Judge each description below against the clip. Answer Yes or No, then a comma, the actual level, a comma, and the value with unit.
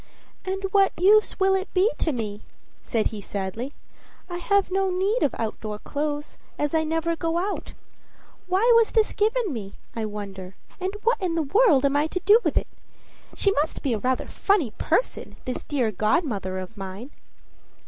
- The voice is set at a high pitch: Yes, very high, 315 Hz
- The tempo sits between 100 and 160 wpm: No, average, 180 wpm